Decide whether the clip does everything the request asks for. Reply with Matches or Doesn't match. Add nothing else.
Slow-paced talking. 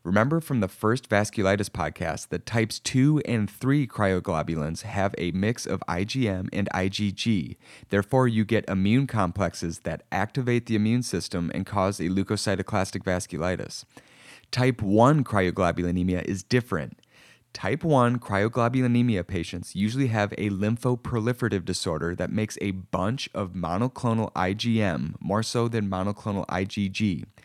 Matches